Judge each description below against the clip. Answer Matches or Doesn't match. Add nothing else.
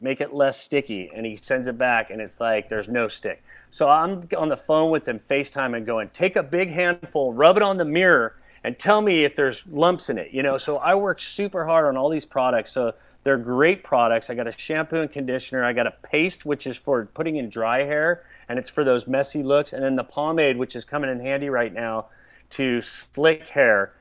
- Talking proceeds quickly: Matches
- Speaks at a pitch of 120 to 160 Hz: Matches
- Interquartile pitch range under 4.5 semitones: Doesn't match